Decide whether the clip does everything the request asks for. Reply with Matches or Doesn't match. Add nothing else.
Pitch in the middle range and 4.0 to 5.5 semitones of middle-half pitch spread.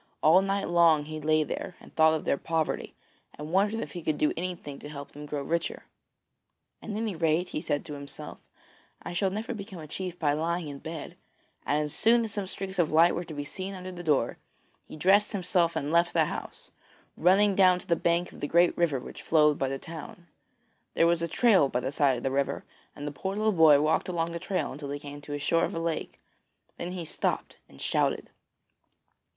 Doesn't match